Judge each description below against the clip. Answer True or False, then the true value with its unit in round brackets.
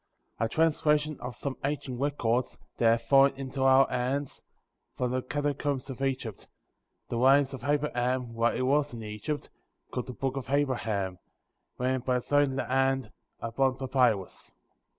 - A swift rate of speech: False (150 wpm)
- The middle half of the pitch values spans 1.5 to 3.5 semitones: True (2.4 semitones)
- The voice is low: True (130 Hz)